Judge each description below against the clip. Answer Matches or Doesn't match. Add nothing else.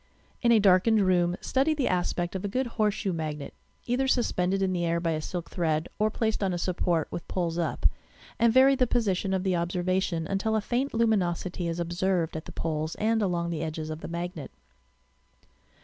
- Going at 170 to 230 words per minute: Matches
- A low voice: Doesn't match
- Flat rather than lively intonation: Doesn't match